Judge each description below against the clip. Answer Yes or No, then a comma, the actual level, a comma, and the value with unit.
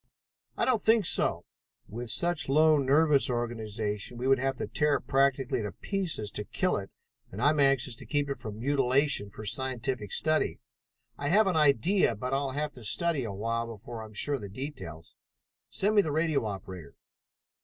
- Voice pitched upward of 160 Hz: No, low, 135 Hz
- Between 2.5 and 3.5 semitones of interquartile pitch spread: No, average, 5.2 semitones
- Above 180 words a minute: Yes, average, 195 wpm